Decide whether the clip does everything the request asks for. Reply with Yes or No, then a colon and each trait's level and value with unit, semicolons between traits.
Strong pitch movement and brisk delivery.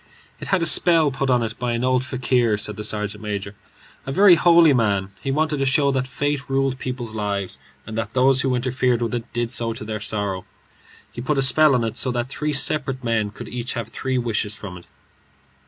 No: average, 3.8 semitones; fast, 220 wpm